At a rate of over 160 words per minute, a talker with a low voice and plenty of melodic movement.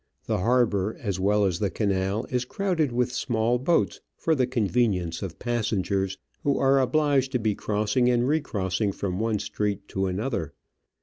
No: average, 170 wpm; low, 110 Hz; average, 4.4 semitones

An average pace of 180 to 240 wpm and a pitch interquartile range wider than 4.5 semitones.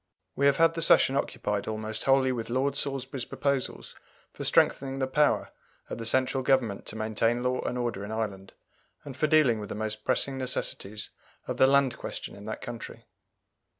No: average, 185 wpm; average, 3.8 semitones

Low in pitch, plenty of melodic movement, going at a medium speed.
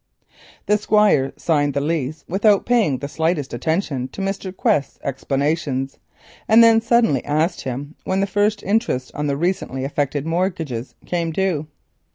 No: medium, 160 Hz; wide, 5.8 semitones; average, 150 wpm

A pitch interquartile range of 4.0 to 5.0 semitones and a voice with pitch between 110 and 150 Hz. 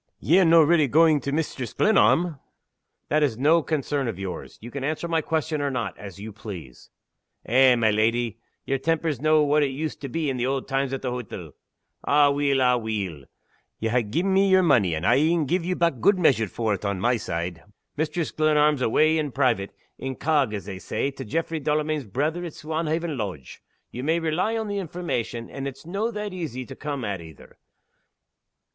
No: wide, 5.5 semitones; medium, 140 Hz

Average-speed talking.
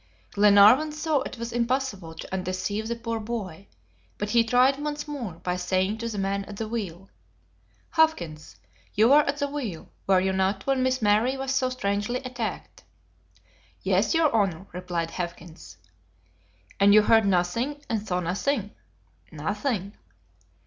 Yes: average, 150 wpm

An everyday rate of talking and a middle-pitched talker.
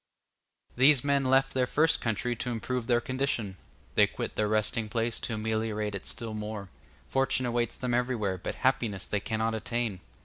No: average, 170 wpm; low, 115 Hz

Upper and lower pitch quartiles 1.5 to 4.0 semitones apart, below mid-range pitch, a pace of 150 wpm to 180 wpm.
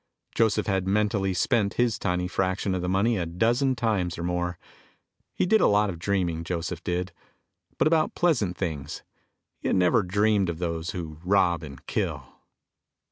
Yes: average, 3.4 semitones; very low, 95 Hz; average, 170 wpm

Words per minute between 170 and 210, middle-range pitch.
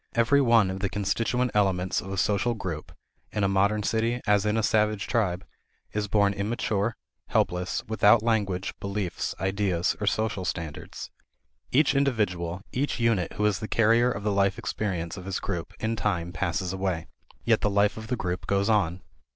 No: average, 175 wpm; low, 100 Hz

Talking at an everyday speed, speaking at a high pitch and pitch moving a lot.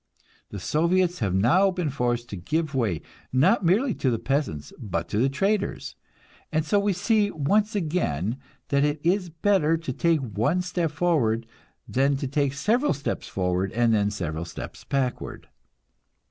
No: average, 160 wpm; medium, 145 Hz; wide, 7.7 semitones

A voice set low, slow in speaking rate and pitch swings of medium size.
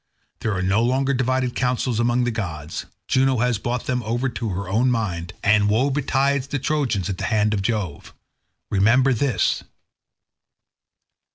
No: low, 120 Hz; average, 160 wpm; average, 4.0 semitones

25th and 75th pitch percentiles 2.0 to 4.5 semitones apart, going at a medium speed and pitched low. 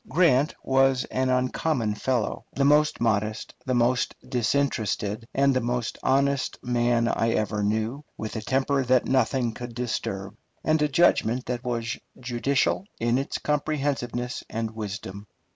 Yes: average, 3.1 semitones; average, 145 wpm; low, 125 Hz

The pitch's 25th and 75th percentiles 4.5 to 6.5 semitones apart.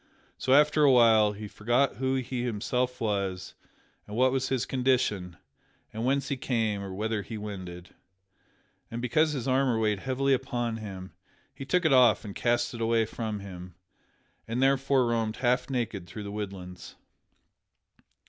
No: average, 4.0 semitones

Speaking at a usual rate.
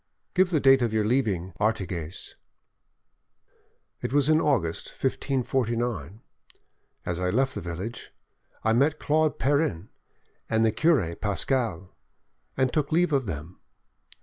No: slow, 125 wpm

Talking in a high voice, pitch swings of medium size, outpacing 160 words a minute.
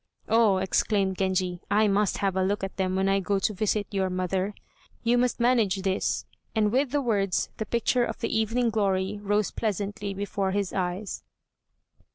No: high, 200 Hz; narrow, 2.3 semitones; average, 180 wpm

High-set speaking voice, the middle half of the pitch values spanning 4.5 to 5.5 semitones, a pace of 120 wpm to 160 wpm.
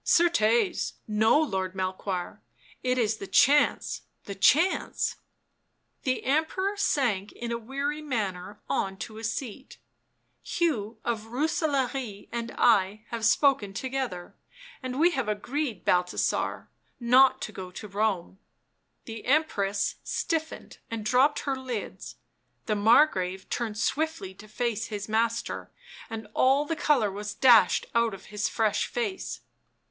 Yes: high, 230 Hz; average, 4.9 semitones; average, 140 wpm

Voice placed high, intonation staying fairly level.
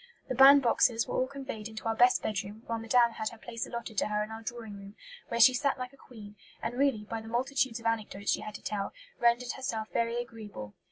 Yes: high, 230 Hz; narrow, 2.3 semitones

